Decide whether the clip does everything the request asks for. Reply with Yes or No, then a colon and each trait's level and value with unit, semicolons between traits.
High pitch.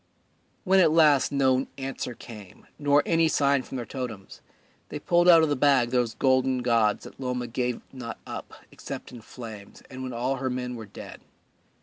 No: low, 130 Hz